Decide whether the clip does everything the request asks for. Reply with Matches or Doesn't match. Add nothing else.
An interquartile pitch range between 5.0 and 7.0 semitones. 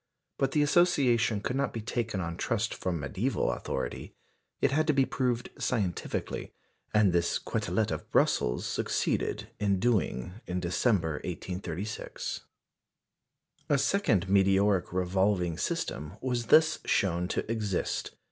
Matches